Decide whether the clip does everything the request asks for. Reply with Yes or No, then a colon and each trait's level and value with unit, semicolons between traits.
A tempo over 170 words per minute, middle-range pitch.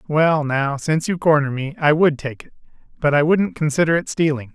Yes: average, 200 wpm; medium, 150 Hz